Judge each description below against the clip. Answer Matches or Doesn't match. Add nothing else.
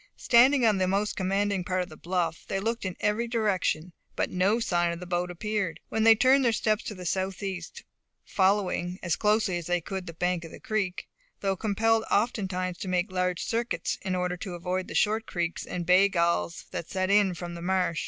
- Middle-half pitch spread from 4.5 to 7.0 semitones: Doesn't match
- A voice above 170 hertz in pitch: Matches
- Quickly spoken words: Matches